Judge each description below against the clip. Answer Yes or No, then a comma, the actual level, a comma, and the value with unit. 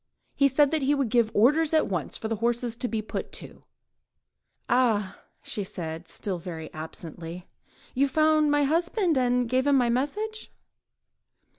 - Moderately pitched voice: No, high, 245 Hz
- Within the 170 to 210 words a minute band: No, average, 160 wpm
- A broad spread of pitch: Yes, wide, 6.1 semitones